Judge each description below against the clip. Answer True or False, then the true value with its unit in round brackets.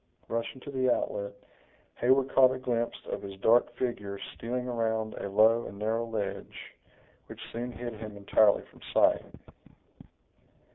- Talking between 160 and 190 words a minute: False (145 wpm)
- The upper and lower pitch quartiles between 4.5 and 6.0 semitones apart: False (2.5 semitones)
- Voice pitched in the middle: False (115 Hz)